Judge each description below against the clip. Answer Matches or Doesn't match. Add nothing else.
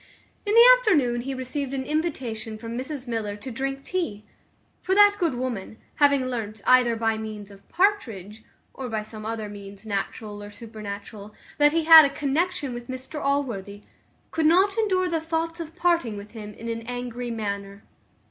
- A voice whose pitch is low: Doesn't match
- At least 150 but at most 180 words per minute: Matches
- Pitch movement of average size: Doesn't match